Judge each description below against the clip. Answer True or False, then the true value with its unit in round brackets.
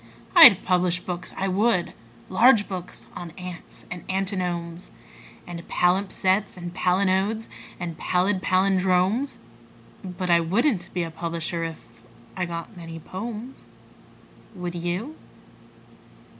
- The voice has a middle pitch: True (180 Hz)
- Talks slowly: True (115 wpm)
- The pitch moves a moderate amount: False (2.0 semitones)